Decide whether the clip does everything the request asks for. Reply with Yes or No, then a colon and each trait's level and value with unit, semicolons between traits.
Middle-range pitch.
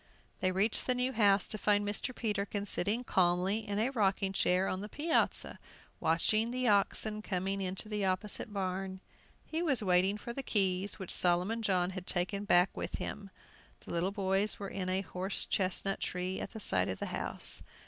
No: high, 195 Hz